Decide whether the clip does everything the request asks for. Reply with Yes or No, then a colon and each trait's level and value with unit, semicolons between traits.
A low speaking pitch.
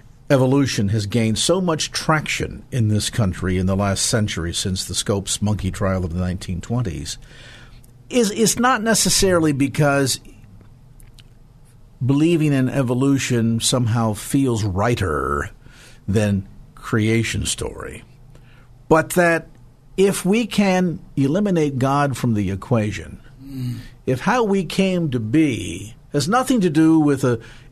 Yes: low, 125 Hz